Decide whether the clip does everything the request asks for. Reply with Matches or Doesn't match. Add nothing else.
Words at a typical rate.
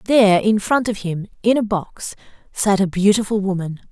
Matches